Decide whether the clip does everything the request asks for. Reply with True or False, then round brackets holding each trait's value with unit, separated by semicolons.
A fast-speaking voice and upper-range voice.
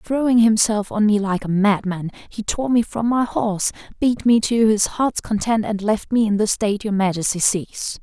True (210 wpm; 215 Hz)